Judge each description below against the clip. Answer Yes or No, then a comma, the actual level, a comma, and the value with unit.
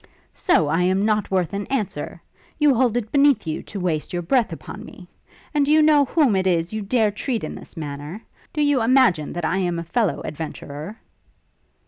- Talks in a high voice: Yes, high, 205 Hz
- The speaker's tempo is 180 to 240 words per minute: Yes, average, 200 wpm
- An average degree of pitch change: No, wide, 7.3 semitones